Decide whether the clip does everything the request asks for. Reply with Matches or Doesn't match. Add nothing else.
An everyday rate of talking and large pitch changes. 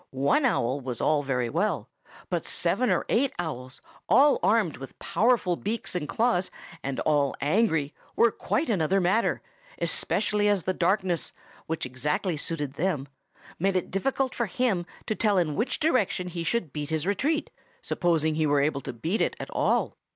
Matches